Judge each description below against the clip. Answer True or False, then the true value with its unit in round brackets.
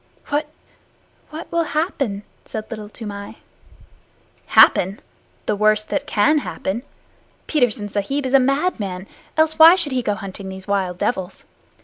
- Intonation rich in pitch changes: True (6.4 semitones)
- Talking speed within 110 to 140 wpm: True (135 wpm)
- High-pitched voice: True (220 Hz)